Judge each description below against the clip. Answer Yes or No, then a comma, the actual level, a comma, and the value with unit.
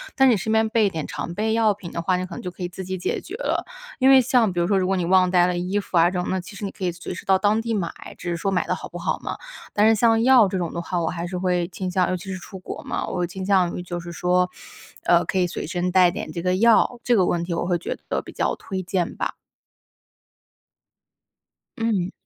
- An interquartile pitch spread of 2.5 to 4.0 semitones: Yes, average, 2.8 semitones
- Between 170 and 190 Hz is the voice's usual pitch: Yes, medium, 185 Hz